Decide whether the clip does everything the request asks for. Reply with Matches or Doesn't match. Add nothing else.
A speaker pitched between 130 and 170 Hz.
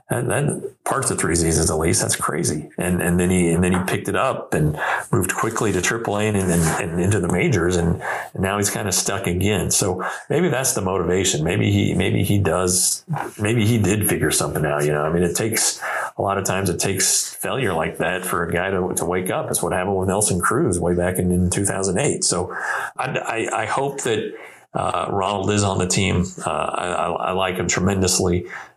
Doesn't match